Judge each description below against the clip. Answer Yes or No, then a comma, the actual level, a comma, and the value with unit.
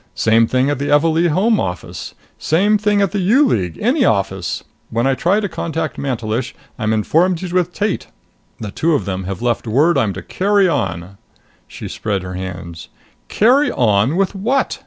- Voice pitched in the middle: Yes, medium, 145 Hz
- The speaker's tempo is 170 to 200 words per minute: Yes, average, 180 wpm